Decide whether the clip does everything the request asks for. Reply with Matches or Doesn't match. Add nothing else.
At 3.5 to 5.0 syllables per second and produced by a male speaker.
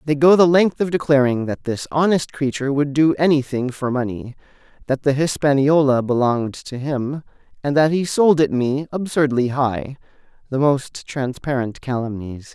Matches